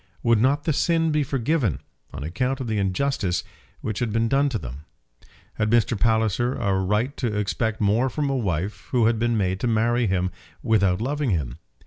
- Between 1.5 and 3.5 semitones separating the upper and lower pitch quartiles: No, average, 4.6 semitones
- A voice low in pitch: Yes, low, 115 Hz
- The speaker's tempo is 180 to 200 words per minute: Yes, average, 190 wpm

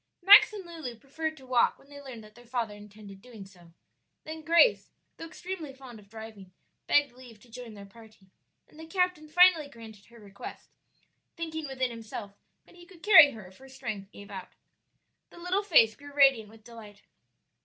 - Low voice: No, very high, 250 Hz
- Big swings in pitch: Yes, wide, 6.7 semitones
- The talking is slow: No, average, 185 wpm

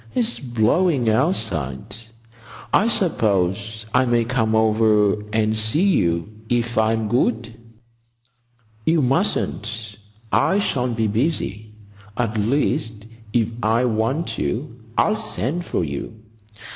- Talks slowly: Yes, slow, 110 wpm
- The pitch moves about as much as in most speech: Yes, average, 3.3 semitones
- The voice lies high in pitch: No, low, 115 Hz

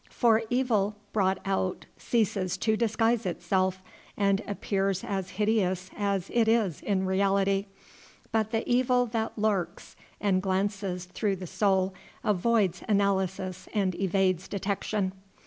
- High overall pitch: Yes, high, 195 Hz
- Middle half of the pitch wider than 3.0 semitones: No, narrow, 2.5 semitones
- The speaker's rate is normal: No, slow, 125 wpm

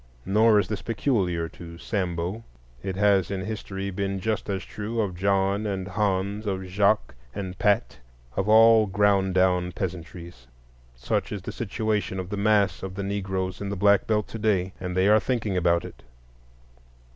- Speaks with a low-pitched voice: Yes, low, 100 Hz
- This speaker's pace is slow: No, average, 170 wpm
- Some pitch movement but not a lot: No, narrow, 2.1 semitones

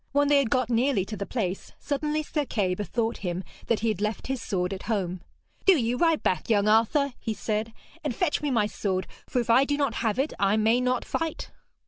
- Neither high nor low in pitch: No, high, 230 Hz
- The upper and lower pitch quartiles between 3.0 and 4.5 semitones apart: No, average, 5.1 semitones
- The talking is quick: Yes, fast, 225 wpm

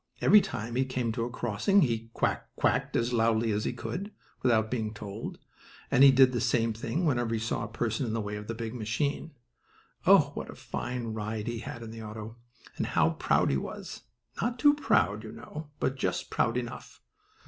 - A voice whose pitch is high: No, low, 115 Hz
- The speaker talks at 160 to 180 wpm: No, fast, 205 wpm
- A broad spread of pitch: No, average, 2.7 semitones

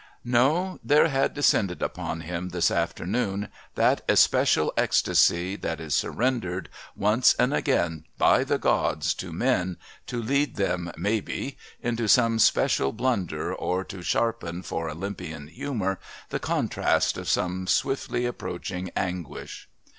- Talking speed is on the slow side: Yes, slow, 130 wpm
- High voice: No, very low, 95 Hz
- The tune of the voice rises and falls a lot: Yes, wide, 5.7 semitones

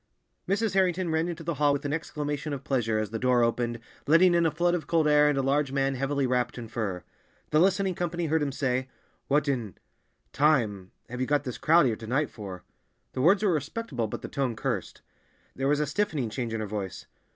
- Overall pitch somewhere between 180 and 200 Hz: No, medium, 140 Hz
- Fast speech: Yes, fast, 215 wpm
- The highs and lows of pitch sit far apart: No, average, 4.8 semitones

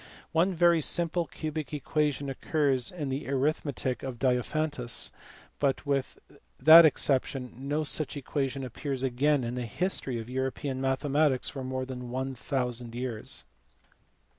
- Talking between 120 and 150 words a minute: Yes, slow, 135 wpm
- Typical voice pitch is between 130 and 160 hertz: Yes, low, 135 Hz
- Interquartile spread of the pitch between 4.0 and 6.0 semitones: No, average, 2.8 semitones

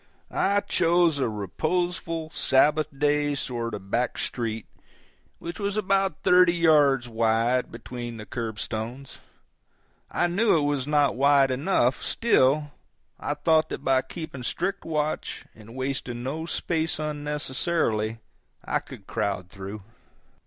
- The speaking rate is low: Yes, slow, 130 wpm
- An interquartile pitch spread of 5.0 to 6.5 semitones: Yes, wide, 5.4 semitones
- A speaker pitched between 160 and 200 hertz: No, medium, 140 Hz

